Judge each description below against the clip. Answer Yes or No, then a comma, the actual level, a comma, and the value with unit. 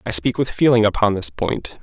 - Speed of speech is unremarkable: No, fast, 230 wpm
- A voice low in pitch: Yes, low, 120 Hz